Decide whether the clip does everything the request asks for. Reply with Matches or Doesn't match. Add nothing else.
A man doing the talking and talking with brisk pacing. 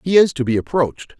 Matches